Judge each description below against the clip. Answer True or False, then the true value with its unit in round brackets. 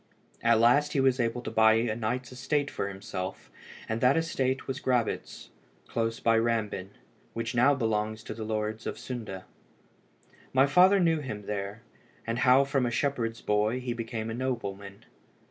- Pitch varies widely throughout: False (3.0 semitones)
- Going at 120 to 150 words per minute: False (165 wpm)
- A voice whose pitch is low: True (115 Hz)